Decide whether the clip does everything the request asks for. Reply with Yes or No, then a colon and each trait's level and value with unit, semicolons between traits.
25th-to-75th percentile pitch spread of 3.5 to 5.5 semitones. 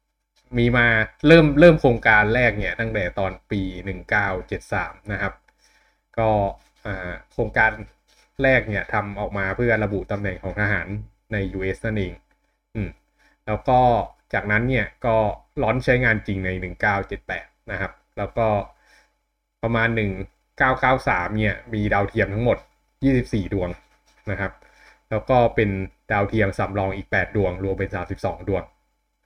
No: average, 3.0 semitones